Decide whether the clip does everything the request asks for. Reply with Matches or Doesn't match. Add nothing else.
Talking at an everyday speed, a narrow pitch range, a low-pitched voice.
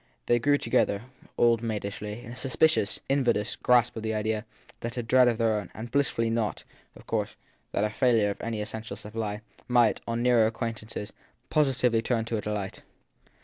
Matches